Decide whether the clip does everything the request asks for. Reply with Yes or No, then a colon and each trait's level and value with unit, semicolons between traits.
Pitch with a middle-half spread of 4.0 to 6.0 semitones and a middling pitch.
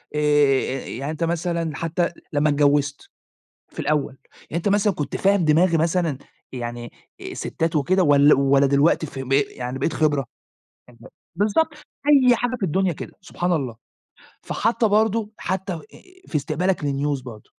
Yes: average, 5.0 semitones; medium, 155 Hz